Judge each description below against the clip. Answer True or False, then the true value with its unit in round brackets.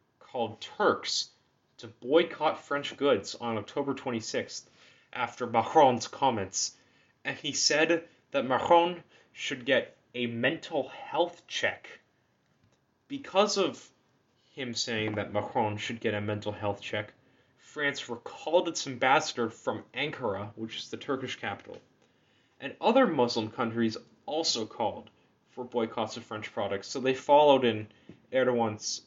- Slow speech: True (130 wpm)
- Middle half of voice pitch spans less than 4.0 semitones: False (4.6 semitones)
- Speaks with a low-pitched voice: True (125 Hz)